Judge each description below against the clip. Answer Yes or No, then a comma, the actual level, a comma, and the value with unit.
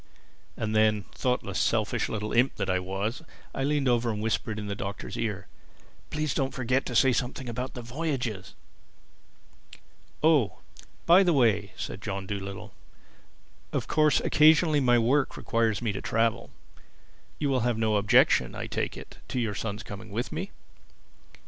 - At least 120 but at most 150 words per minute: No, average, 160 wpm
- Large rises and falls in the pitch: No, average, 4.2 semitones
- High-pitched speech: No, low, 115 Hz